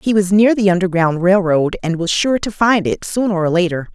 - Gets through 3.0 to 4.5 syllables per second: No, 5.3 syllables/s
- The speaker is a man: No, female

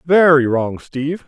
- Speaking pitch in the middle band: Yes, medium, 150 Hz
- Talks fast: No, average, 140 wpm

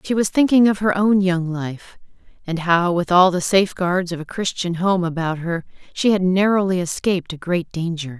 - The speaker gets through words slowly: No, average, 200 wpm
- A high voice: No, medium, 180 Hz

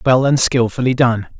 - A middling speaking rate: Yes, average, 170 wpm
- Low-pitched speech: Yes, low, 125 Hz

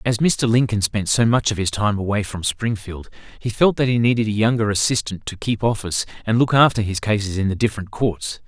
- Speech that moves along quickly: Yes, fast, 225 wpm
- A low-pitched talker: Yes, low, 110 Hz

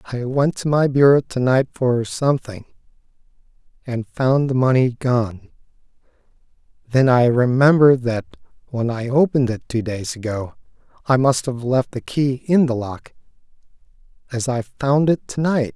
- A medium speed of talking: Yes, average, 150 wpm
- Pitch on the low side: Yes, low, 130 Hz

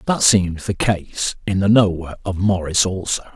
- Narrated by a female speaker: No, male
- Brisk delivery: No, average, 180 wpm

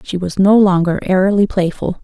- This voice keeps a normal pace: Yes, average, 175 wpm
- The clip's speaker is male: No, female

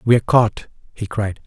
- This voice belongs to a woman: No, male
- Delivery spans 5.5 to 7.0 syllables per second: No, 4.7 syllables/s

